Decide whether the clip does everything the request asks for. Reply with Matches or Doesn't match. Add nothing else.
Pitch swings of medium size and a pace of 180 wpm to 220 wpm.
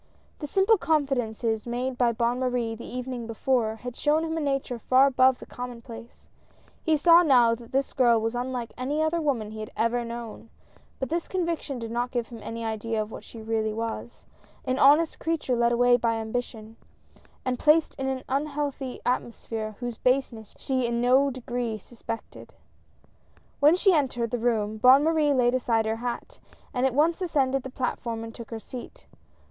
Matches